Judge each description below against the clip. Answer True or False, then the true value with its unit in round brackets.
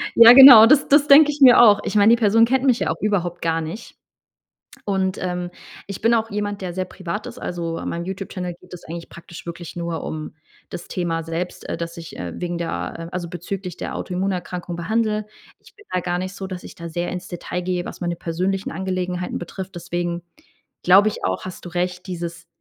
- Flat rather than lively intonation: False (3.0 semitones)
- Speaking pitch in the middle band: True (180 Hz)